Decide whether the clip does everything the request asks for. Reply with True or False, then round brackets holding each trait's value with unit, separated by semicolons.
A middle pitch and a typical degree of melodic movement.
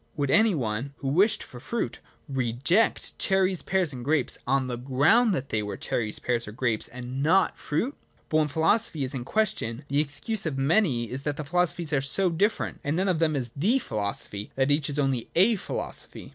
False (145 Hz; 6.0 semitones)